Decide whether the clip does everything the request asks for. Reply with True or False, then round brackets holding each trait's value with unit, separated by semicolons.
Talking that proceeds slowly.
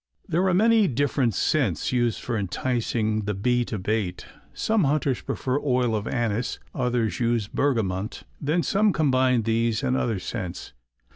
False (150 wpm)